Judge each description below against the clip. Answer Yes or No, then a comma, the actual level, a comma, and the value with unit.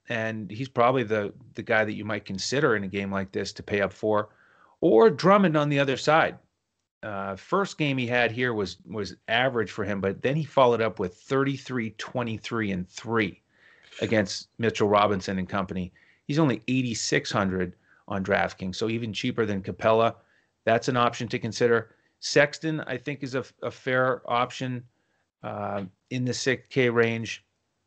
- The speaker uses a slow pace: No, average, 170 wpm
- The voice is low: Yes, low, 115 Hz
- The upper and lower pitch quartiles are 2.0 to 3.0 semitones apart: No, average, 3.7 semitones